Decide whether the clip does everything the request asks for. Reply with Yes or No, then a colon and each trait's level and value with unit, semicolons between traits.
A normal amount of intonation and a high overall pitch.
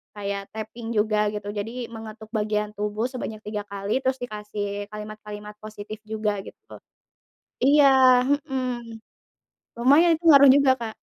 Yes: average, 3.6 semitones; high, 215 Hz